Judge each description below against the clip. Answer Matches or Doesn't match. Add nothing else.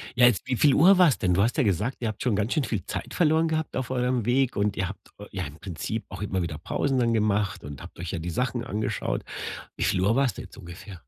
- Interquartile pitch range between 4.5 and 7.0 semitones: Matches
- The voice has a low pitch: Matches